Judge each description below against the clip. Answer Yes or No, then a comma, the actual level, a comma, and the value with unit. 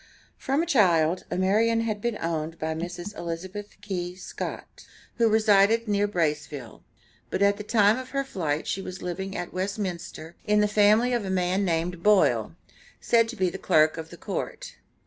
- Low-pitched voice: No, high, 190 Hz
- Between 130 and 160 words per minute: No, average, 175 wpm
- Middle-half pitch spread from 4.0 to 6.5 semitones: No, average, 3.6 semitones